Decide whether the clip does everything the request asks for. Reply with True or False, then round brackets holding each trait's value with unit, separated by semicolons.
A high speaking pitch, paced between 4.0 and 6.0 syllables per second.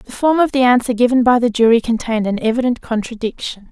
False (235 Hz; 6.3 syllables/s)